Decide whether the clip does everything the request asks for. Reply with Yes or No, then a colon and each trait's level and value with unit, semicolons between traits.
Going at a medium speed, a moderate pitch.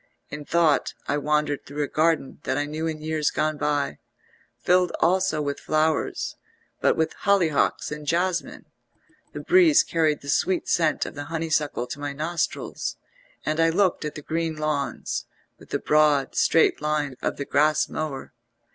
Yes: average, 165 wpm; medium, 155 Hz